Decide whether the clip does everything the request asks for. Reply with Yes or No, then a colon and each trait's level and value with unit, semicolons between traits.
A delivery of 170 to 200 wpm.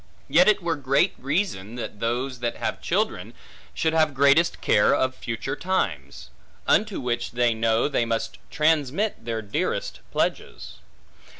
No: average, 140 wpm